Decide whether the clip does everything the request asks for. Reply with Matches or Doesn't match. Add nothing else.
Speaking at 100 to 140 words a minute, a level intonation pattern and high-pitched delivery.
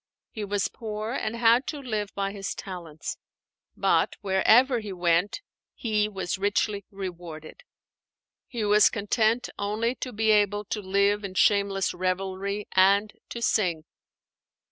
Matches